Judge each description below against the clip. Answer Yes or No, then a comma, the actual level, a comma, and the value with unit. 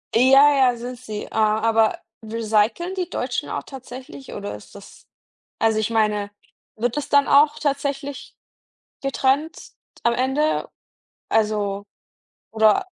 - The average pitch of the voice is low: No, high, 240 Hz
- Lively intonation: No, average, 4.5 semitones